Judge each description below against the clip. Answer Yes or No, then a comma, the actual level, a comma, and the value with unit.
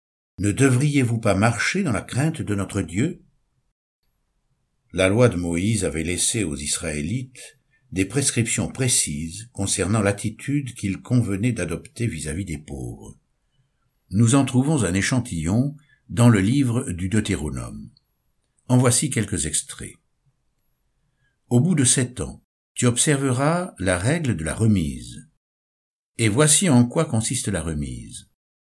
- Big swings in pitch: Yes, wide, 6.7 semitones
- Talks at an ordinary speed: No, slow, 135 wpm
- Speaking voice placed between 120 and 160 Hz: No, low, 110 Hz